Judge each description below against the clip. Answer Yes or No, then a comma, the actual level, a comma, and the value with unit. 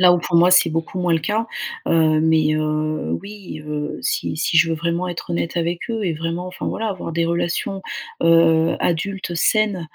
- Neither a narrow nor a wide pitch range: No, narrow, 2.2 semitones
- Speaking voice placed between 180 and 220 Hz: No, medium, 170 Hz